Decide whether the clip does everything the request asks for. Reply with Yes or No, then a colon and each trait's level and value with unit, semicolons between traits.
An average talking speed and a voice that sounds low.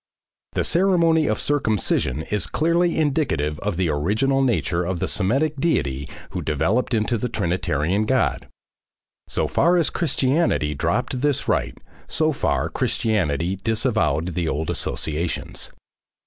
No: slow, 130 wpm; low, 110 Hz